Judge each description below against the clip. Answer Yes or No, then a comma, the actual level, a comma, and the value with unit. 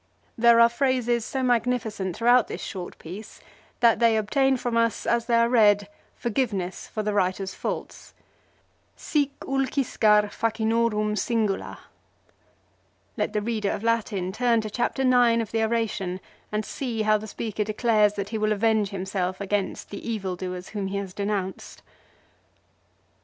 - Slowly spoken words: No, average, 145 wpm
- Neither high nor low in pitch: No, high, 220 Hz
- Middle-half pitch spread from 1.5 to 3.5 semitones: Yes, narrow, 2.6 semitones